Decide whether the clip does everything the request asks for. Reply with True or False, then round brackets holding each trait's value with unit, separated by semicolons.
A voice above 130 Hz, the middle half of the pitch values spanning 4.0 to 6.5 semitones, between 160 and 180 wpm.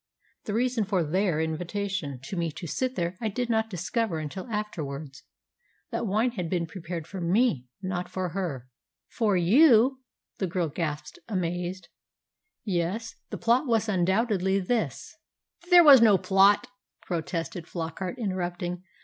False (190 Hz; 4.6 semitones; 145 wpm)